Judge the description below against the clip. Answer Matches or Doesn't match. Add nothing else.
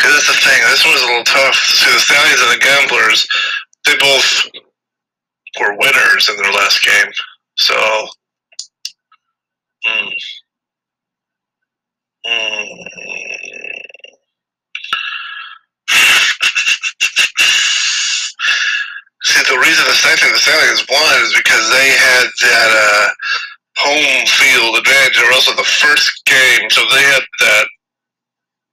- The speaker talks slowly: Matches